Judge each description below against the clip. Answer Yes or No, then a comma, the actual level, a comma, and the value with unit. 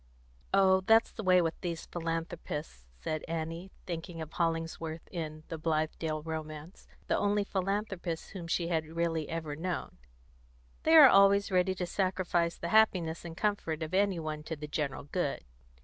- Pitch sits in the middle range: Yes, medium, 170 Hz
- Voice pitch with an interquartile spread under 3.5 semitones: Yes, average, 2.9 semitones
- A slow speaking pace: No, average, 160 wpm